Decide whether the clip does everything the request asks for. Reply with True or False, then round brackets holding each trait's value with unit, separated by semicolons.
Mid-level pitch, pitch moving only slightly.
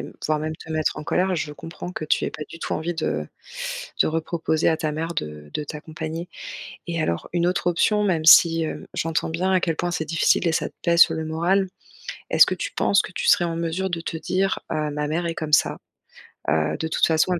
True (165 Hz; 1.9 semitones)